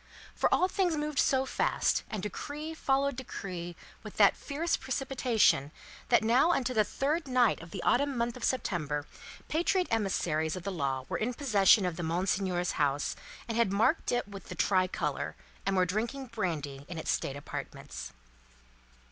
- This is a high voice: Yes, high, 215 Hz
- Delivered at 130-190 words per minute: Yes, average, 165 wpm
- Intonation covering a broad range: Yes, wide, 7.4 semitones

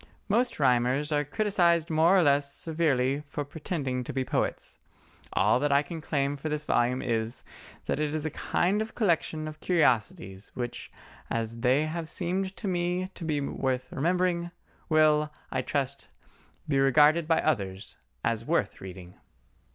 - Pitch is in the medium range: Yes, medium, 150 Hz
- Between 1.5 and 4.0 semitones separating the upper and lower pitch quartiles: No, average, 4.6 semitones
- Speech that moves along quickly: No, average, 160 wpm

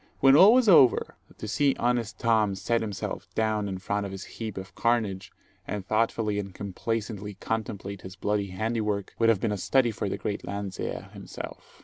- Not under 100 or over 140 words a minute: No, average, 185 wpm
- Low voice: Yes, low, 105 Hz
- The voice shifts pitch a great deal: No, narrow, 2.5 semitones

